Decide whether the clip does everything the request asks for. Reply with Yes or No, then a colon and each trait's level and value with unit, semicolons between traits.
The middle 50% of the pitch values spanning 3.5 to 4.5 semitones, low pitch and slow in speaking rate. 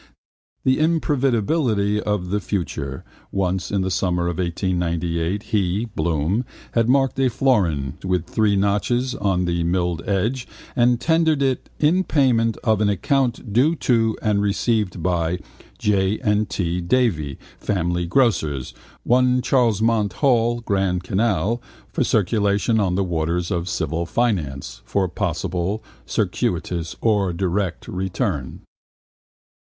No: average, 5.0 semitones; low, 100 Hz; slow, 130 wpm